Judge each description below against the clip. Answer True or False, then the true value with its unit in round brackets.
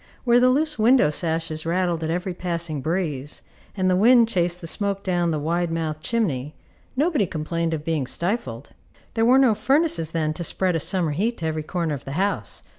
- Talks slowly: False (195 wpm)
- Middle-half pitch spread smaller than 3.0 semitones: False (4.8 semitones)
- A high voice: False (175 Hz)